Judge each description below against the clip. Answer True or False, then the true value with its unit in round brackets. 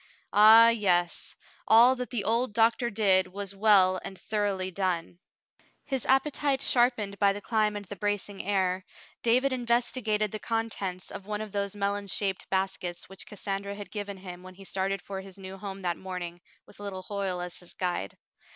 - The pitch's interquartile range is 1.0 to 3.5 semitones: True (2.4 semitones)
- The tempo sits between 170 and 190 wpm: True (175 wpm)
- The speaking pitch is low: False (200 Hz)